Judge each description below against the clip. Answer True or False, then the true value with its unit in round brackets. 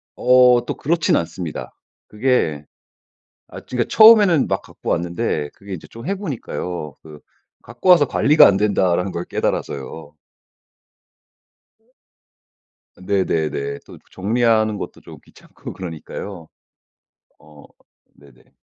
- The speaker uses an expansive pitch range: True (7.8 semitones)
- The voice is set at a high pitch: False (100 Hz)